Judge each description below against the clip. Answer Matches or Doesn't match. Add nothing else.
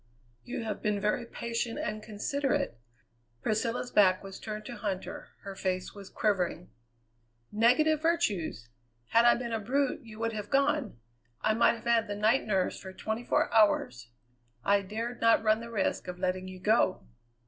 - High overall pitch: Matches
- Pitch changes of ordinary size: Matches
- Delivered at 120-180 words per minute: Matches